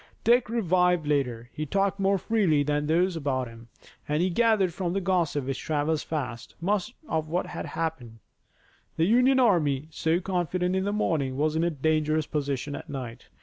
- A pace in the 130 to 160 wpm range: No, average, 180 wpm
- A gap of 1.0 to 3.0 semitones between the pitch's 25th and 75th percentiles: No, average, 4.5 semitones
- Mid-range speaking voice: Yes, medium, 160 Hz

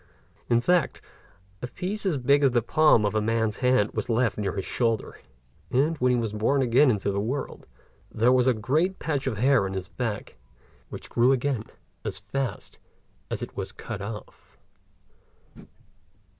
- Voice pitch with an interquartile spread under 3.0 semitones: No, average, 4.3 semitones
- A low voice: Yes, low, 120 Hz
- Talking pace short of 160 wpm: No, average, 170 wpm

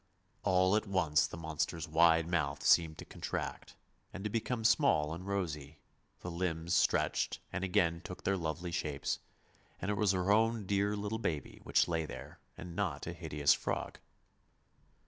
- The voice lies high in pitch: No, very low, 85 Hz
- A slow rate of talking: No, average, 165 wpm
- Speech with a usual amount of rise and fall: Yes, average, 3.6 semitones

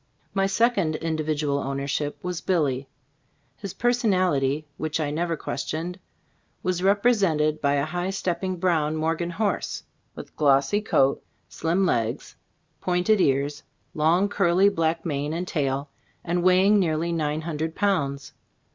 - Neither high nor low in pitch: Yes, medium, 165 Hz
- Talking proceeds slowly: Yes, slow, 130 wpm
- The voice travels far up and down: No, average, 3.8 semitones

